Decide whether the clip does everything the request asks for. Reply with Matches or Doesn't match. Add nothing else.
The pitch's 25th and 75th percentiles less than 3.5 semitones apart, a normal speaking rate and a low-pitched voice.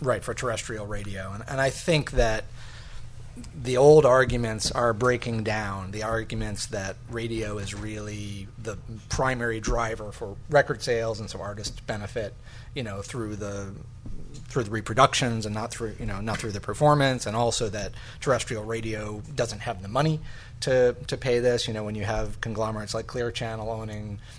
Matches